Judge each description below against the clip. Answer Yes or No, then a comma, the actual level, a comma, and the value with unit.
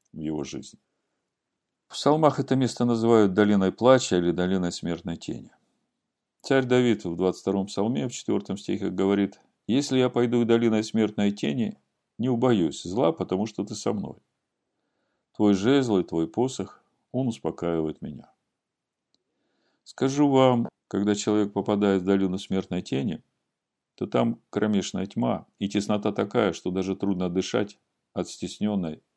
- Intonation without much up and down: No, average, 4.2 semitones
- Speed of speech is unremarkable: Yes, average, 140 wpm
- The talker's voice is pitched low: Yes, low, 105 Hz